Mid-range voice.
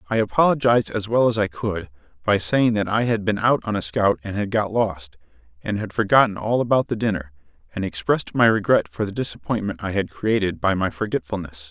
No: low, 100 Hz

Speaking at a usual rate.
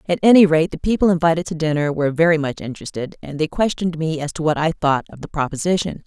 No: fast, 240 wpm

